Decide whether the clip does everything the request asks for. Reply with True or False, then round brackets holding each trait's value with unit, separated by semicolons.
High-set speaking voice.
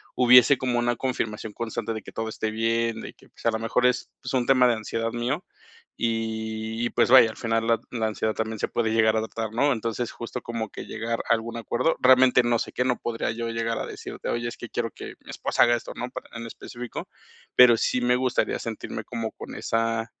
False (115 Hz)